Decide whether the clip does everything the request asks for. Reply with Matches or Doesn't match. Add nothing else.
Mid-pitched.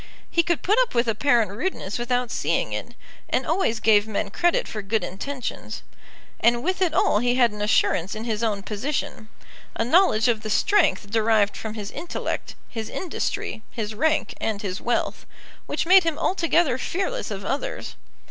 Doesn't match